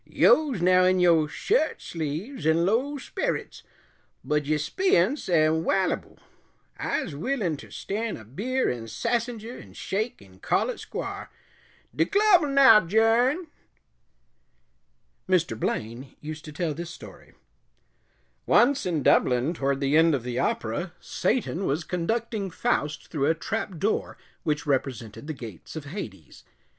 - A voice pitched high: No, medium, 170 Hz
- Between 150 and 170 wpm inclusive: No, average, 140 wpm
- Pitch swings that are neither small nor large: No, wide, 7.7 semitones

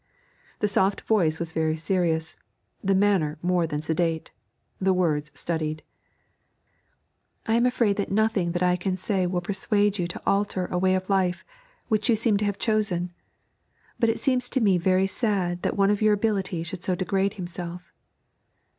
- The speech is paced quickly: No, average, 170 wpm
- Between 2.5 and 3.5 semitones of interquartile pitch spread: Yes, average, 2.8 semitones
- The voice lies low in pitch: No, medium, 185 Hz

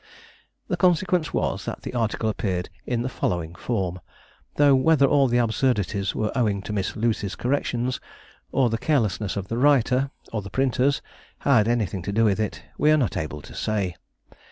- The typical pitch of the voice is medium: No, low, 115 Hz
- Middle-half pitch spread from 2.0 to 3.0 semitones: No, average, 4.9 semitones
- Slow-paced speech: No, average, 180 wpm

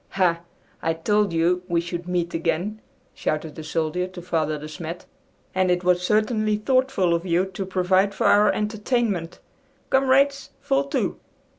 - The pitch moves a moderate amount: Yes, average, 4.0 semitones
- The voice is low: No, medium, 180 Hz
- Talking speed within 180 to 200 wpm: No, average, 155 wpm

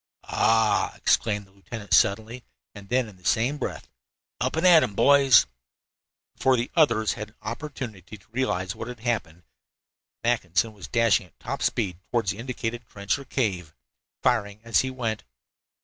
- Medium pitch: No, low, 115 Hz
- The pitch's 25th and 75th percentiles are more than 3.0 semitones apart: Yes, average, 3.6 semitones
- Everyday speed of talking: Yes, average, 165 wpm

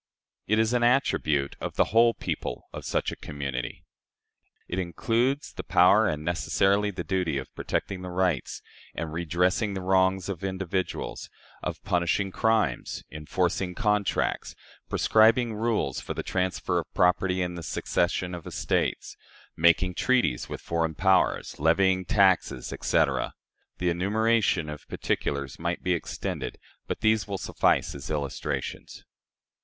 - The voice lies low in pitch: Yes, very low, 90 Hz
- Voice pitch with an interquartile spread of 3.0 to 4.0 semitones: Yes, average, 3.6 semitones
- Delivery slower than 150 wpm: Yes, average, 140 wpm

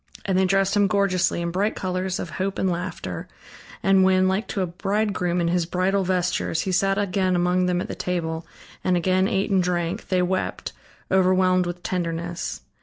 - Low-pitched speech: No, medium, 185 Hz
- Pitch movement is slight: Yes, narrow, 1.4 semitones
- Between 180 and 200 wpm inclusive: Yes, average, 185 wpm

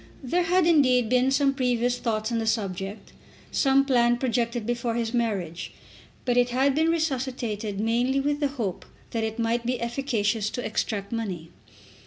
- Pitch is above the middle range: Yes, high, 240 Hz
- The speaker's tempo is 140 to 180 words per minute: Yes, average, 165 wpm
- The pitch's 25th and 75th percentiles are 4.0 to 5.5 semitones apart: No, average, 3.2 semitones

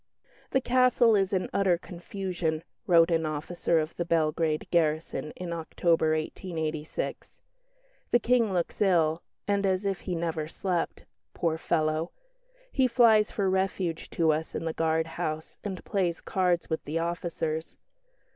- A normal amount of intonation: Yes, average, 3.1 semitones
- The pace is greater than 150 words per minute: No, average, 145 wpm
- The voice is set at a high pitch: No, medium, 170 Hz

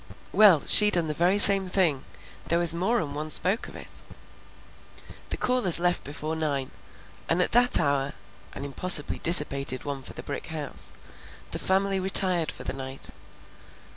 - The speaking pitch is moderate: Yes, medium, 170 Hz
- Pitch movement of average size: Yes, average, 4.9 semitones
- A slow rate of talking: No, average, 160 wpm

